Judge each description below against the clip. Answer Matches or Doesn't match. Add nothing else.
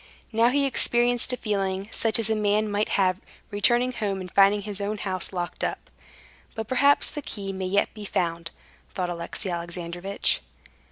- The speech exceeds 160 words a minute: Matches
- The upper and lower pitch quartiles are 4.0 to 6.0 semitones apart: Doesn't match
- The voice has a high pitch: Matches